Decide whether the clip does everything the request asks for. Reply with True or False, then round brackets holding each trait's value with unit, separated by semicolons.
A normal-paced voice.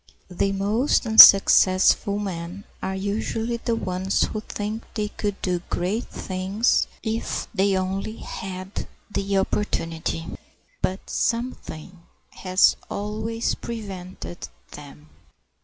False (105 wpm)